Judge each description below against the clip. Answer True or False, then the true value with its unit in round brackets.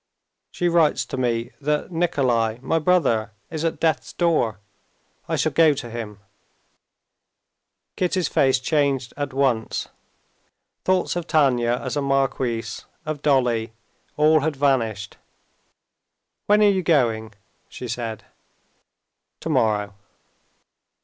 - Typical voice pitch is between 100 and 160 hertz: True (135 Hz)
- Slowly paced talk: True (115 wpm)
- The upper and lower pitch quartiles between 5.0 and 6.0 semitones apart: True (5.5 semitones)